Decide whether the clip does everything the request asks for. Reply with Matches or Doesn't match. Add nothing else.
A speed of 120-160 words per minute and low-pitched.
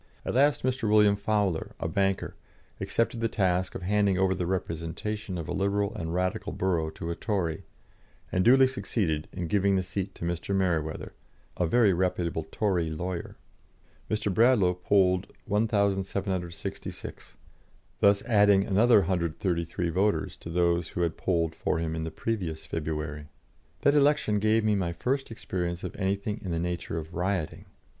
Matches